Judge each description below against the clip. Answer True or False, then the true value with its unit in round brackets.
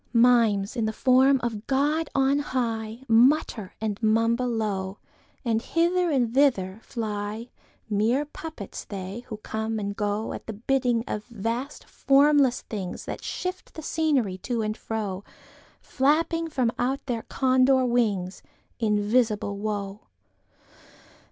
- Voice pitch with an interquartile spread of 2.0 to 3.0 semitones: False (4.0 semitones)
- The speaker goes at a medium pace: False (105 wpm)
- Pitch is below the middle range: False (230 Hz)